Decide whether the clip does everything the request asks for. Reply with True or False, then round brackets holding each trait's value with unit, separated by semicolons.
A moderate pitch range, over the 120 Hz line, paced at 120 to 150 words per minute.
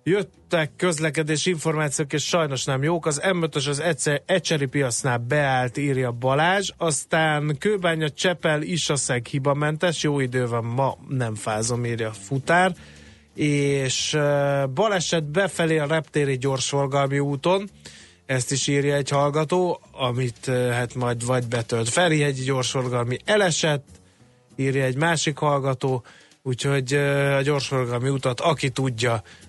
True (3.7 semitones; 140 Hz; 130 wpm)